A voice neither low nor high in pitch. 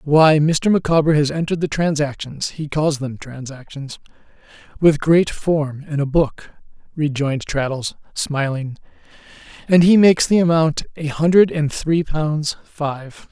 Yes: medium, 150 Hz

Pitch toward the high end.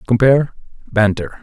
No: low, 115 Hz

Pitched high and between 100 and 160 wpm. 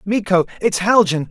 Yes: high, 195 Hz; average, 140 wpm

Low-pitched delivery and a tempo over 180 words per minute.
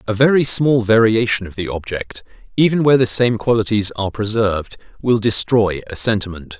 No: low, 110 Hz; average, 165 wpm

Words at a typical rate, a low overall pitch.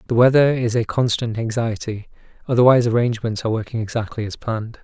Yes: average, 160 wpm; low, 115 Hz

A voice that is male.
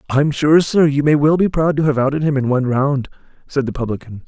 Yes: male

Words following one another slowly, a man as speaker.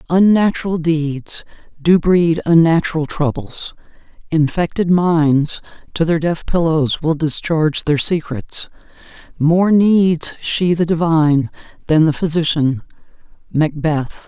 No: slow, 105 wpm; female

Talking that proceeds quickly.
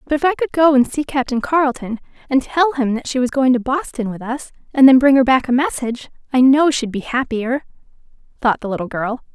Yes: fast, 230 wpm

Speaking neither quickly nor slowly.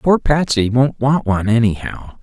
Yes: average, 160 wpm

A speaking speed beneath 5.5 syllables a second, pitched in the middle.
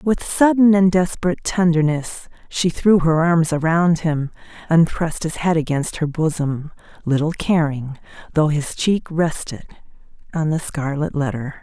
Yes: 4.4 syllables/s; medium, 160 Hz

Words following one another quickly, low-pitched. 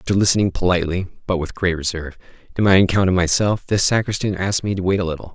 Yes: fast, 225 wpm; very low, 95 Hz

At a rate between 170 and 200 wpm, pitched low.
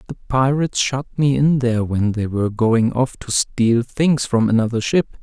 Yes: average, 195 wpm; low, 125 Hz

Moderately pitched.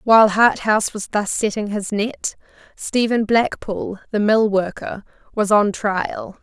No: high, 210 Hz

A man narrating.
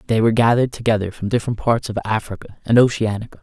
Yes: male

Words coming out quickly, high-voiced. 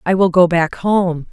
No: fast, 225 wpm; medium, 175 Hz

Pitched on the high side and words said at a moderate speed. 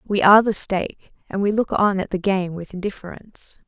No: high, 195 Hz; fast, 210 wpm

